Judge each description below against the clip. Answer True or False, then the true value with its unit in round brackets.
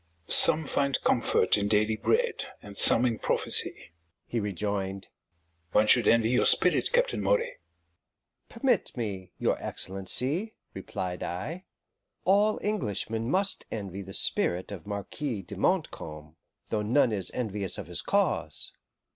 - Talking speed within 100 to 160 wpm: True (135 wpm)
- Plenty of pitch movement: True (8.5 semitones)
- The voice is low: True (110 Hz)